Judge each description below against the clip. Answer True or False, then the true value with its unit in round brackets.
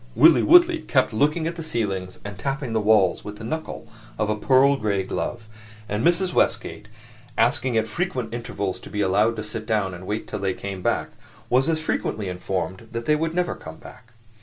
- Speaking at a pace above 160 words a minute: True (200 wpm)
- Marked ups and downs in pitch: True (5.8 semitones)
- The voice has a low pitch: True (110 Hz)